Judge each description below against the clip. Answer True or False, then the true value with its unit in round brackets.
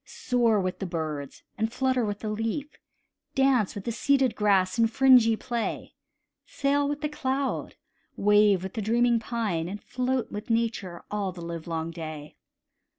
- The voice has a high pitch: True (220 Hz)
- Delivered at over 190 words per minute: False (155 wpm)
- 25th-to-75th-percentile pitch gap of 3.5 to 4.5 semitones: False (5.1 semitones)